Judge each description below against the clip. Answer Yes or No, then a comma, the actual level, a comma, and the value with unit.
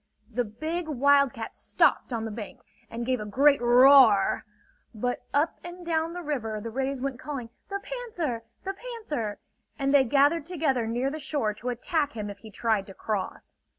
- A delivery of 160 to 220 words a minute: Yes, average, 180 wpm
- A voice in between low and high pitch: No, very high, 265 Hz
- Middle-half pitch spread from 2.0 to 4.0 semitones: No, average, 5.2 semitones